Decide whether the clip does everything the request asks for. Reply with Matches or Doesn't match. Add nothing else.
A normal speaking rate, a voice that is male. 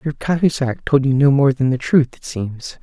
Doesn't match